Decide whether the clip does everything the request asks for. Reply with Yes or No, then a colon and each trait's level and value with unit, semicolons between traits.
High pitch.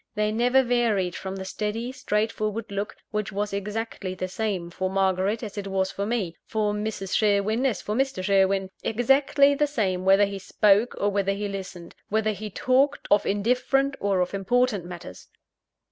Yes: high, 205 Hz